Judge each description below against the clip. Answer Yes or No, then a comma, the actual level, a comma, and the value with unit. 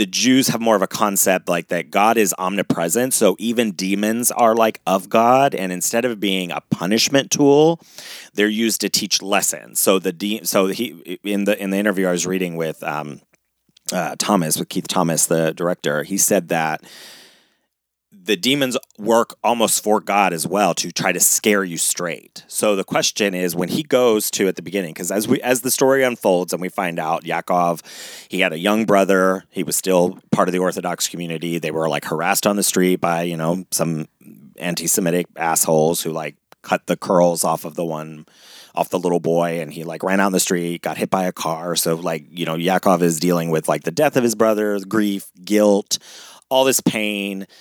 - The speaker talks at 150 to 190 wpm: No, fast, 205 wpm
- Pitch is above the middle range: No, very low, 95 Hz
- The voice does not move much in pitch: No, average, 3.7 semitones